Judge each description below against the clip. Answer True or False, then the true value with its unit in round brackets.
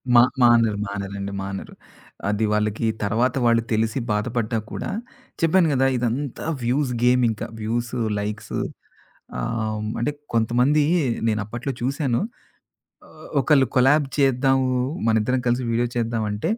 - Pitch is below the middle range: True (120 Hz)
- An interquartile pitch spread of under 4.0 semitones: True (3.2 semitones)